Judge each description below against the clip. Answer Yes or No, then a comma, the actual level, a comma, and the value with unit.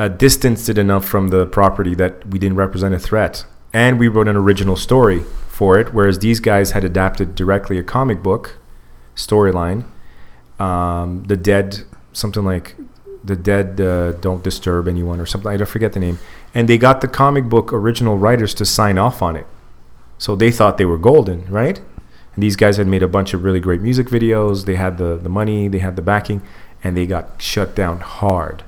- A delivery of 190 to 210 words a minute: Yes, average, 200 wpm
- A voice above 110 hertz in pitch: No, very low, 95 Hz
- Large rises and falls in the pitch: No, average, 2.7 semitones